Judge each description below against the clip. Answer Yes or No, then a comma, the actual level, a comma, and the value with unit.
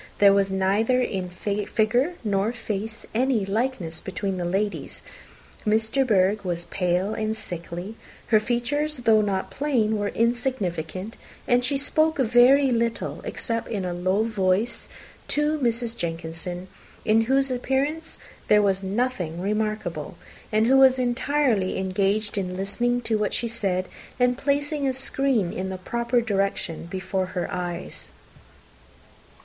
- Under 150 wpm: Yes, average, 140 wpm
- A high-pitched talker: Yes, high, 215 Hz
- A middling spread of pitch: Yes, average, 4.6 semitones